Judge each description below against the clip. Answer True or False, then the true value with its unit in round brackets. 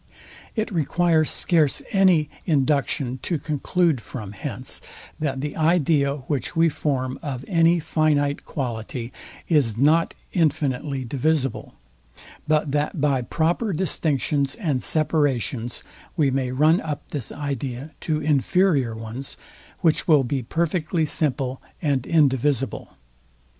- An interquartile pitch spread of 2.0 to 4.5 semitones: True (3.3 semitones)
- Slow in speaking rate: True (115 wpm)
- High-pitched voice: False (145 Hz)